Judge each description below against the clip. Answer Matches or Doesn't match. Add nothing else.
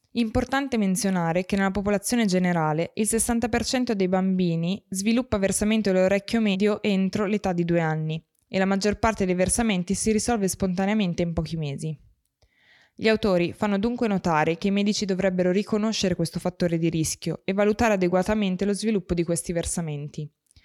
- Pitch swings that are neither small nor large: Matches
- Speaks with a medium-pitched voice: Doesn't match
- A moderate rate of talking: Matches